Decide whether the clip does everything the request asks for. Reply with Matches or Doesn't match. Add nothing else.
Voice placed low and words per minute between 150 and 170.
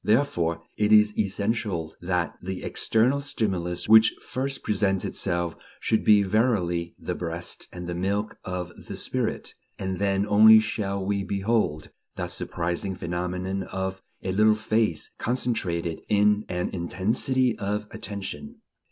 Doesn't match